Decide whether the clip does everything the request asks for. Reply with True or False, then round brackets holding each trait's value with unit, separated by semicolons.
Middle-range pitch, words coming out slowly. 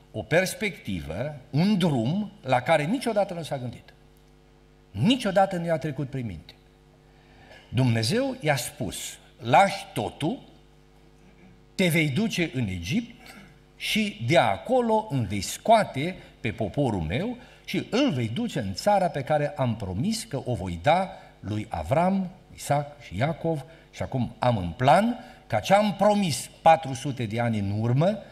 False (150 Hz; 145 wpm)